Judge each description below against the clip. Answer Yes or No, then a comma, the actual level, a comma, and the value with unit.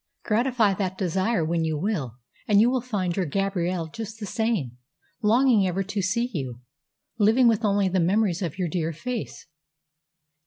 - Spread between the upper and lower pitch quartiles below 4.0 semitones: No, average, 4.5 semitones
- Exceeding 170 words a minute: No, average, 165 wpm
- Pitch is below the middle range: No, high, 195 Hz